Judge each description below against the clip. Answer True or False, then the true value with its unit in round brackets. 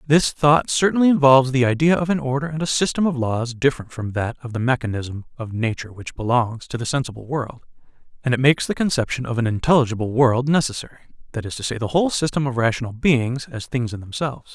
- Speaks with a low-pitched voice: True (130 Hz)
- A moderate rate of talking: False (215 wpm)